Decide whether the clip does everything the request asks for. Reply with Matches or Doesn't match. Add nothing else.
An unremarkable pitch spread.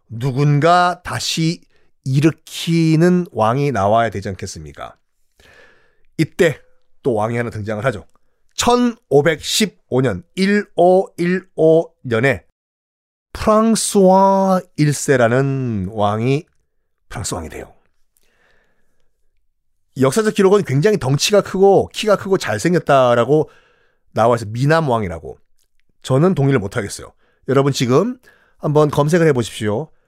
Doesn't match